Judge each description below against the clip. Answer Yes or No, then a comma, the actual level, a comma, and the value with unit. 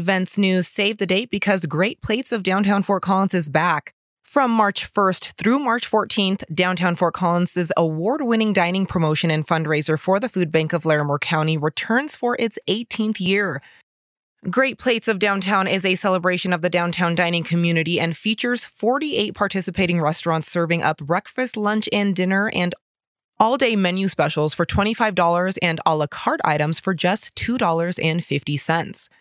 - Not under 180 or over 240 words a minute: No, average, 160 wpm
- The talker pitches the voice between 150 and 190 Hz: Yes, medium, 185 Hz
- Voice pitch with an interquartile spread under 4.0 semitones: Yes, average, 3.6 semitones